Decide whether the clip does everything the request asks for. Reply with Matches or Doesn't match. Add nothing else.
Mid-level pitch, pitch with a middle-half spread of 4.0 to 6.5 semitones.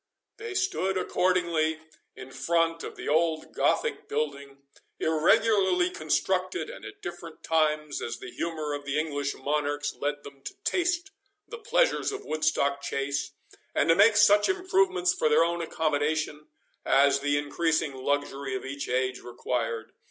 Matches